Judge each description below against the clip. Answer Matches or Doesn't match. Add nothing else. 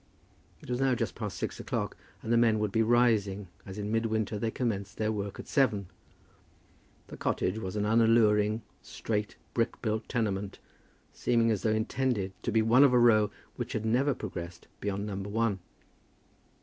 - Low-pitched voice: Matches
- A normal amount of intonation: Doesn't match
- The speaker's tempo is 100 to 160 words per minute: Doesn't match